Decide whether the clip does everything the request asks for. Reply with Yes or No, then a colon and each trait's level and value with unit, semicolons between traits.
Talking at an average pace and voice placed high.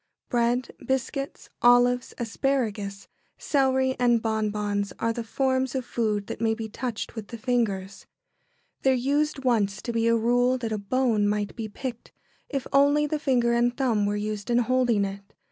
Yes: average, 170 wpm; high, 235 Hz